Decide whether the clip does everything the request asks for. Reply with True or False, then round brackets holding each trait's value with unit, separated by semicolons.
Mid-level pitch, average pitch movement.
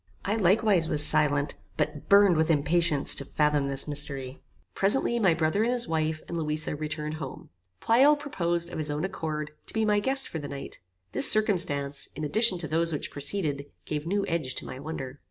True (155 Hz; 4.8 semitones)